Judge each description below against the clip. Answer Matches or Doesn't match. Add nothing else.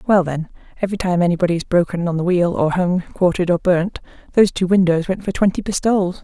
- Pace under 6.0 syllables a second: Doesn't match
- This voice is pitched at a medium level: Matches